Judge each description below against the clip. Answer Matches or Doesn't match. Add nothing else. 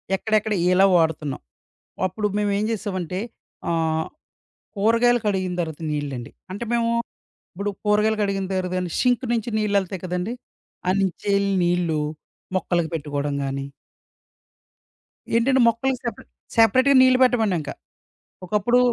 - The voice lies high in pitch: Matches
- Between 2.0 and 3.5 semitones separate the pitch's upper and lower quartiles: Doesn't match